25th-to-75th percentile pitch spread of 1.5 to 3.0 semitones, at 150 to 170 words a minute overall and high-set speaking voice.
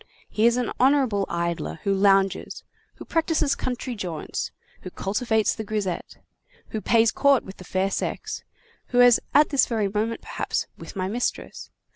No: average, 4.1 semitones; average, 160 wpm; high, 220 Hz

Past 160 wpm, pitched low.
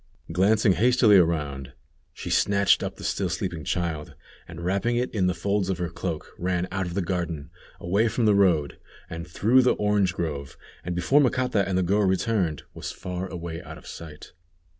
Yes: average, 185 wpm; very low, 90 Hz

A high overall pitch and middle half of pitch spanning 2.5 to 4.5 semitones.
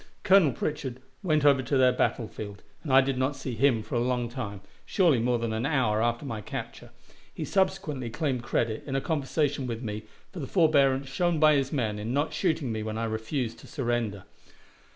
No: low, 130 Hz; average, 4.1 semitones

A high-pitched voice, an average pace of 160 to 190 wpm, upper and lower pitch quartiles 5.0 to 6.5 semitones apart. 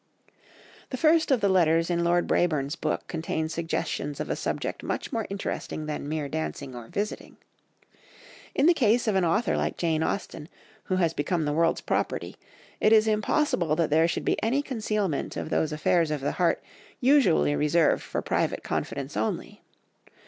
No: medium, 170 Hz; average, 170 wpm; wide, 5.5 semitones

